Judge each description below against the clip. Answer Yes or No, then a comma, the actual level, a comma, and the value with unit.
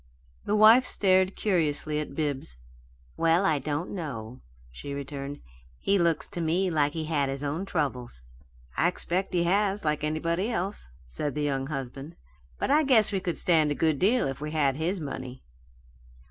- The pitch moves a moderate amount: Yes, average, 4.7 semitones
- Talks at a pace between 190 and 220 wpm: No, average, 175 wpm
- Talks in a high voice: No, medium, 155 Hz